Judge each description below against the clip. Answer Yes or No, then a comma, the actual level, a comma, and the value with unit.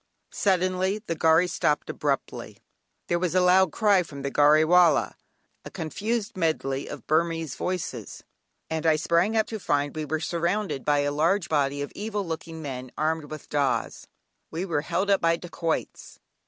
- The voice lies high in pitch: No, medium, 165 Hz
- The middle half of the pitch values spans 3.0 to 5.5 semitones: Yes, average, 3.7 semitones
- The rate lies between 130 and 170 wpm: Yes, average, 165 wpm